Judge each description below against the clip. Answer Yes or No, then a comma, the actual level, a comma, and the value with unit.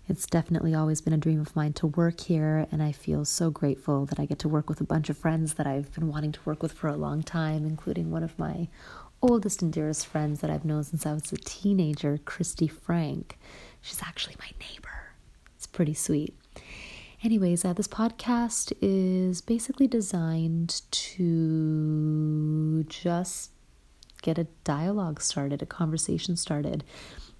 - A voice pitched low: No, medium, 160 Hz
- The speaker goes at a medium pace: Yes, average, 170 wpm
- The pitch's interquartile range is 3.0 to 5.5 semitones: No, narrow, 2.4 semitones